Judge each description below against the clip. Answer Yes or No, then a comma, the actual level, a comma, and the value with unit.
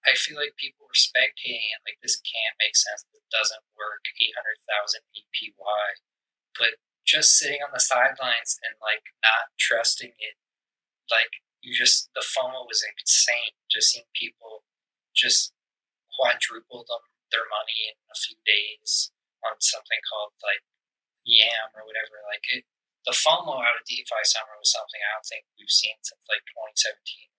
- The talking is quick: No, average, 165 wpm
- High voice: Yes, very high, 290 Hz